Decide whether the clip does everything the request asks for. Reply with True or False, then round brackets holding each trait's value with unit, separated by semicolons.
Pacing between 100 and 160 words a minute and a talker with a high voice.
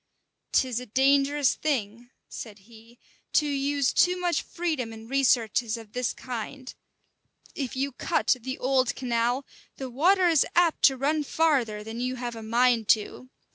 True (155 wpm; 255 Hz)